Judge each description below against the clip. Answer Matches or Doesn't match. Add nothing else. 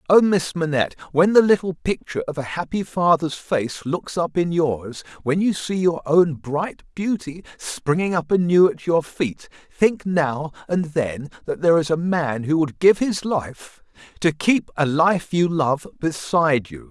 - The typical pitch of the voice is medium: Matches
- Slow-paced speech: Doesn't match